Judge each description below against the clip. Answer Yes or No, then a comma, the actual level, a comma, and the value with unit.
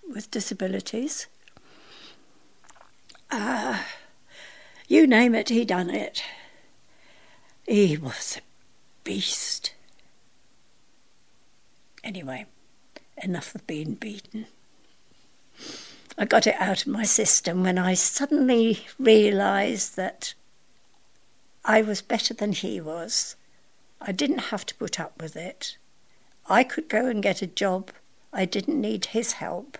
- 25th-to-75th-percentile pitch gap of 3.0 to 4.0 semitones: Yes, average, 3.5 semitones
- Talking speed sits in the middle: No, slow, 115 wpm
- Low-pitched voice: No, high, 215 Hz